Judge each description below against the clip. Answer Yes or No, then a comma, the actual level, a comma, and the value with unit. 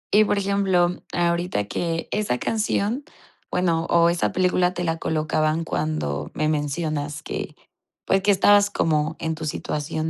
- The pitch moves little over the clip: No, average, 3.2 semitones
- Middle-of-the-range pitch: Yes, medium, 165 Hz